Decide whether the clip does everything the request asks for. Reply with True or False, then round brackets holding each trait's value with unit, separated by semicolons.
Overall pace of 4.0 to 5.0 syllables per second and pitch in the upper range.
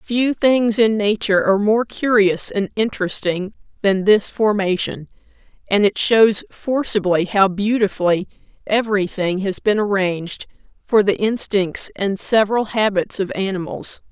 True (4.5 syllables/s; 205 Hz)